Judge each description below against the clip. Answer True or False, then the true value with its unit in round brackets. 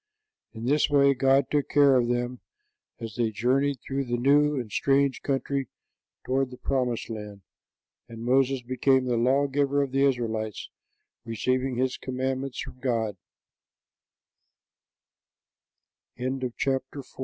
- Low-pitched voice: True (130 Hz)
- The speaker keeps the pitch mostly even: True (2.2 semitones)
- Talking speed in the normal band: False (115 wpm)